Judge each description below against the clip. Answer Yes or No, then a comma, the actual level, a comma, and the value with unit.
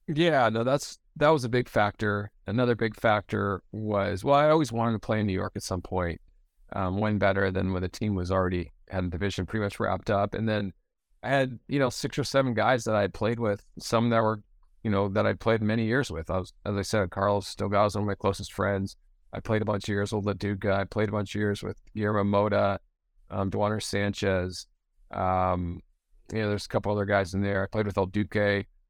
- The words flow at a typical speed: No, fast, 235 wpm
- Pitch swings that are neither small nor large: No, narrow, 2.3 semitones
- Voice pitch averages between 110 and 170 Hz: No, low, 100 Hz